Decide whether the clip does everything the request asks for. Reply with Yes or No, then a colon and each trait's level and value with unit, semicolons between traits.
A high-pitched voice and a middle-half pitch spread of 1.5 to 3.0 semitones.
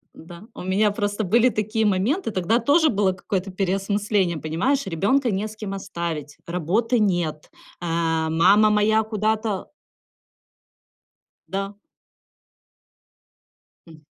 No: high, 200 Hz; average, 3.7 semitones